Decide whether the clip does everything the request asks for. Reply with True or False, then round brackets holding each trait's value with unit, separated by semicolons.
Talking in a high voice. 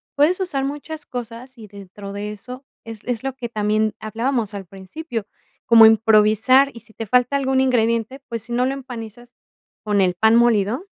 True (230 Hz)